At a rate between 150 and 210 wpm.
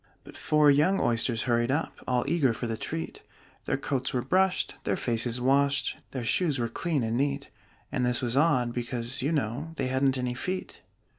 Yes: average, 190 wpm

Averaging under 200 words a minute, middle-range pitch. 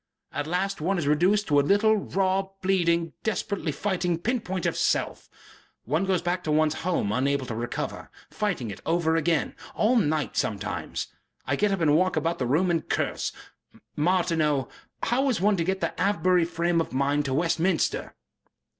Yes: average, 175 wpm; medium, 170 Hz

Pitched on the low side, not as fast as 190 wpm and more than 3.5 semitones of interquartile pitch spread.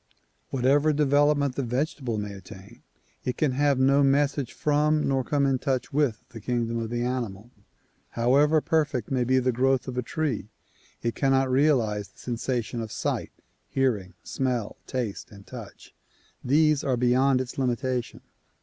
No: low, 130 Hz; average, 155 wpm; average, 3.1 semitones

